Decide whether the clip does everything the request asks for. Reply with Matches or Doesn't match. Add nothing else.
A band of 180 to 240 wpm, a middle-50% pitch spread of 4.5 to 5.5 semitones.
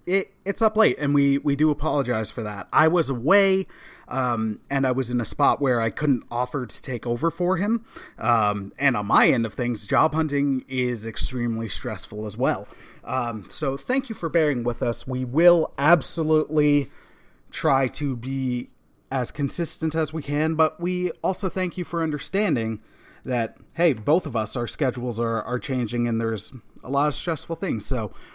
Matches